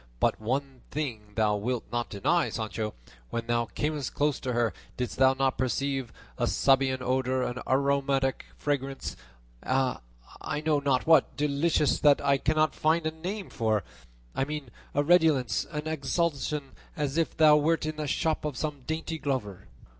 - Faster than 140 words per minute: Yes, average, 160 wpm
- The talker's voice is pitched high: No, medium, 140 Hz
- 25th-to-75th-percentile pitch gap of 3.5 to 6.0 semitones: No, average, 3.1 semitones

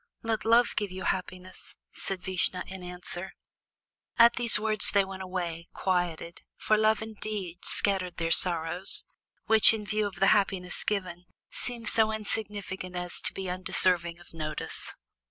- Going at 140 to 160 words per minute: Yes, average, 150 wpm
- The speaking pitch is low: No, high, 190 Hz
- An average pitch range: Yes, average, 3.0 semitones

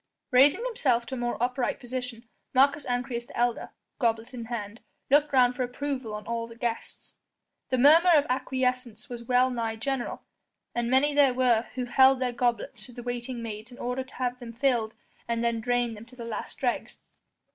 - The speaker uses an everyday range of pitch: No, narrow, 1.8 semitones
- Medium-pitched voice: No, high, 245 Hz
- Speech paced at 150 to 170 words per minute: No, average, 190 wpm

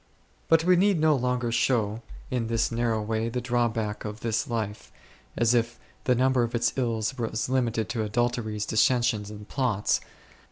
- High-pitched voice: No, low, 115 Hz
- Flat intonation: Yes, narrow, 2.2 semitones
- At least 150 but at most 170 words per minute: Yes, average, 165 wpm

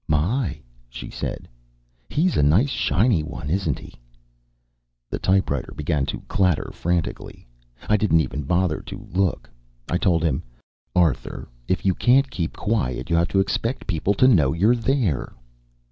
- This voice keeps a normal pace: Yes, average, 150 wpm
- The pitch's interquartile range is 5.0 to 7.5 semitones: Yes, wide, 5.5 semitones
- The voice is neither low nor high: No, very low, 90 Hz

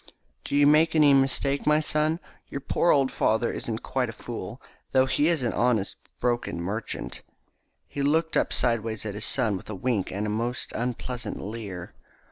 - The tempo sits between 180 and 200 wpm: Yes, average, 185 wpm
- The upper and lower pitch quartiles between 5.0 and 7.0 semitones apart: No, average, 4.5 semitones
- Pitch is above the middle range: No, low, 125 Hz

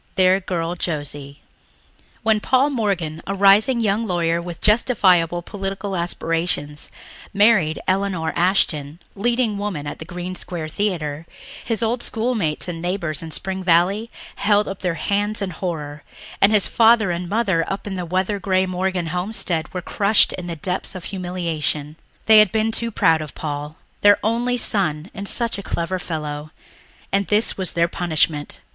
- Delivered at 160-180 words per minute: Yes, average, 165 wpm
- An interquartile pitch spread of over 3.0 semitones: Yes, average, 3.8 semitones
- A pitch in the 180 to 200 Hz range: Yes, medium, 185 Hz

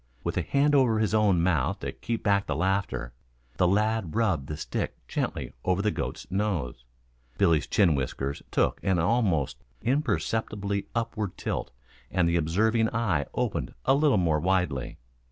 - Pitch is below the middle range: Yes, very low, 95 Hz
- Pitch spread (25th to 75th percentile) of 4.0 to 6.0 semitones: Yes, average, 5.2 semitones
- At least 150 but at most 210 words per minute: Yes, average, 155 wpm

